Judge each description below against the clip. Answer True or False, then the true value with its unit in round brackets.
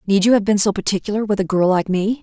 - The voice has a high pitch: True (200 Hz)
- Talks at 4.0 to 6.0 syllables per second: False (6.6 syllables/s)